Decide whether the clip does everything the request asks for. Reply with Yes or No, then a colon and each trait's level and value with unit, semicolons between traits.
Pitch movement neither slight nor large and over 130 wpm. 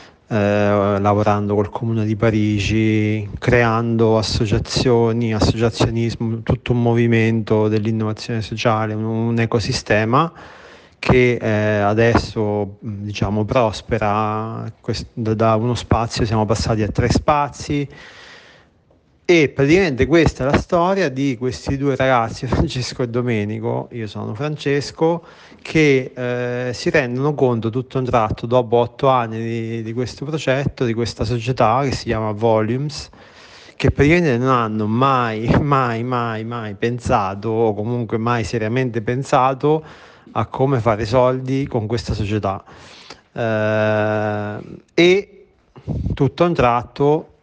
No: average, 3.1 semitones; slow, 115 wpm